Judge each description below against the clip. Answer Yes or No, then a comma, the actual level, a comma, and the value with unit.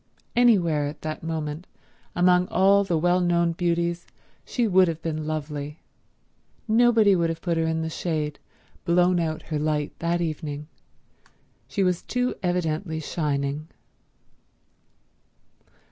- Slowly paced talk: Yes, slow, 130 wpm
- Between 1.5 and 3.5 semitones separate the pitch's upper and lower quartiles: Yes, narrow, 2.6 semitones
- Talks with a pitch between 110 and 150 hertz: No, medium, 165 Hz